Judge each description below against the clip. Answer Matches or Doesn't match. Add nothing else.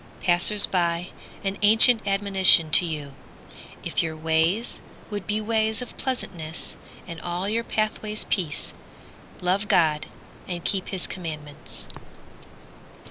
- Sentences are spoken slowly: Matches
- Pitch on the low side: Doesn't match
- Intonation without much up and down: Doesn't match